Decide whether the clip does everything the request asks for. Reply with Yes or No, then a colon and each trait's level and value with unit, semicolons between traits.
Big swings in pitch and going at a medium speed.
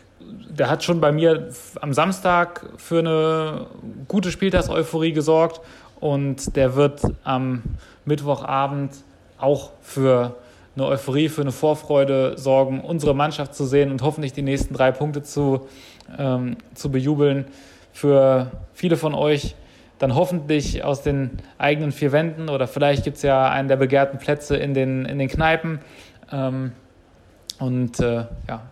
No: narrow, 2.4 semitones; average, 140 wpm